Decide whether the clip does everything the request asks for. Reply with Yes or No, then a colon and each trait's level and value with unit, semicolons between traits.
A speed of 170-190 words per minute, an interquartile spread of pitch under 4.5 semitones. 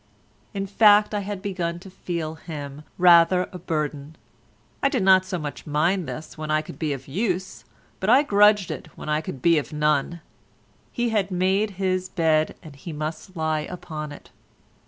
Yes: average, 180 wpm; average, 3.8 semitones